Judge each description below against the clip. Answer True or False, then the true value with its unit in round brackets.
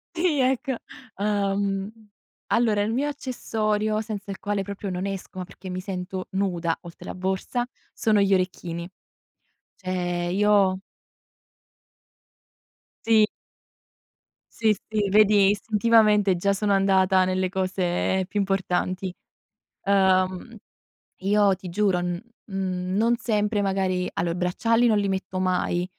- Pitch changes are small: True (2.2 semitones)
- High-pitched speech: True (195 Hz)